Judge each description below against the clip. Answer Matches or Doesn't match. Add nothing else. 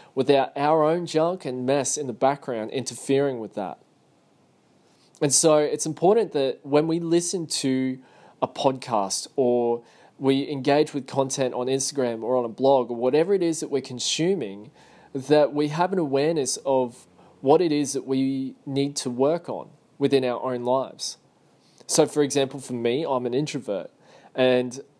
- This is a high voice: Doesn't match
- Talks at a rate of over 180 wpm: Doesn't match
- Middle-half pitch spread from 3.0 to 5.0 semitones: Doesn't match